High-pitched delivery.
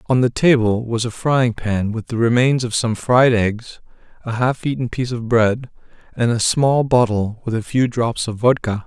No: low, 120 Hz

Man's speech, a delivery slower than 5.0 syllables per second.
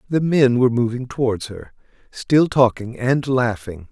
Yes: male; 4.5 syllables/s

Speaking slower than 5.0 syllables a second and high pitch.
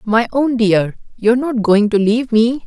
Yes: 4.8 syllables/s; high, 230 Hz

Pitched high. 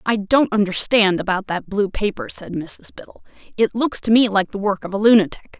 Yes: high, 205 Hz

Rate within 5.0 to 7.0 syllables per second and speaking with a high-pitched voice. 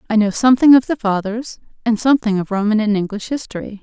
Yes: 6.5 syllables/s; high, 220 Hz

